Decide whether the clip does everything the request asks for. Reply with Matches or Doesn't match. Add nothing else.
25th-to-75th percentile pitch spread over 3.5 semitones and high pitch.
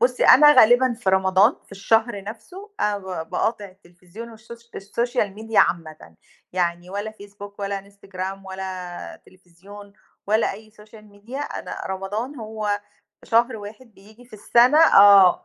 Doesn't match